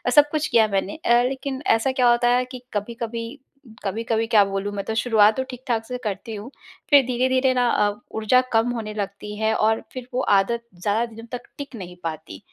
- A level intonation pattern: No, average, 3.2 semitones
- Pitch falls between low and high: No, high, 230 Hz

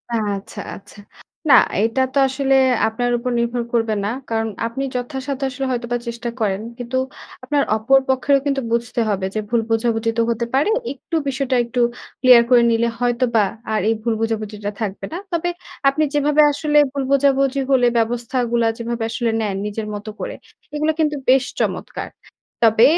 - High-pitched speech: Yes, high, 240 Hz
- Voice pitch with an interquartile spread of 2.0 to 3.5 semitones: Yes, average, 3.1 semitones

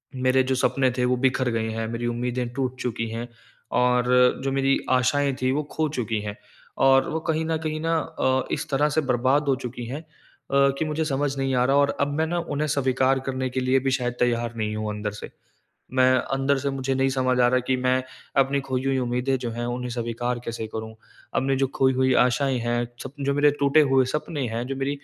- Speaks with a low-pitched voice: Yes, low, 130 Hz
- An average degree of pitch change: No, narrow, 2.0 semitones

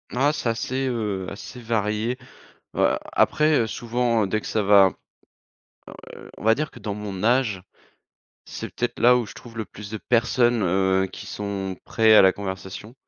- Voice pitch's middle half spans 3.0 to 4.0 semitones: Yes, average, 3.3 semitones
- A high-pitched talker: No, low, 110 Hz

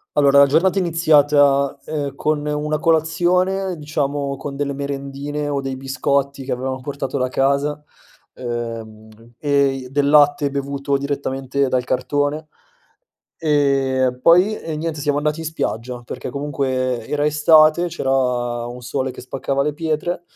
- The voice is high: No, medium, 140 Hz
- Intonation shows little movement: Yes, narrow, 2.1 semitones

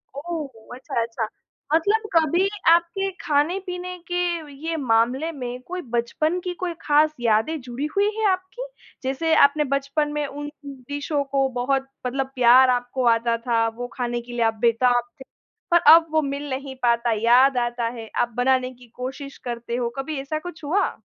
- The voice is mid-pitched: No, very high, 275 Hz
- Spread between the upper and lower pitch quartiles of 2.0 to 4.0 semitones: No, average, 4.6 semitones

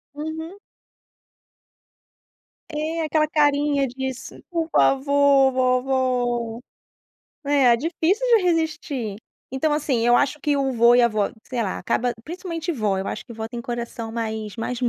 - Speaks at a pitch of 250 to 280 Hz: Yes, very high, 265 Hz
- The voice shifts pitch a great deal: No, average, 4.3 semitones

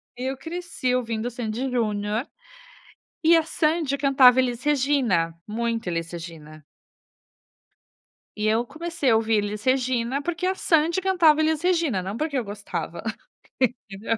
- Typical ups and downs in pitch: No, wide, 6.2 semitones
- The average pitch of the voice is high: Yes, very high, 250 Hz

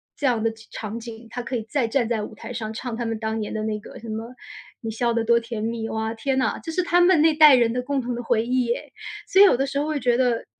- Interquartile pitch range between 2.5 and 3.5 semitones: Yes, average, 2.9 semitones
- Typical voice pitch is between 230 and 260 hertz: Yes, high, 235 Hz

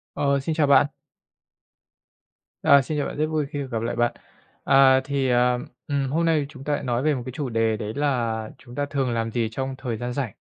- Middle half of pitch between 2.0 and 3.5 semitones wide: Yes, average, 3.1 semitones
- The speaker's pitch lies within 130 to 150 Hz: Yes, low, 135 Hz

